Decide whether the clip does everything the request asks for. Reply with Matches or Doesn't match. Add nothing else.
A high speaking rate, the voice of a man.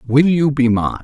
Matches